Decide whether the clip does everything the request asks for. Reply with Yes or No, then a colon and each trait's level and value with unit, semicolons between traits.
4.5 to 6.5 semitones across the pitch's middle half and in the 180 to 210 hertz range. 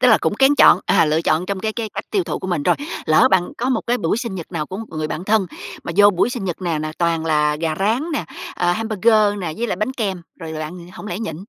Yes: average, 5.2 semitones; high, 190 Hz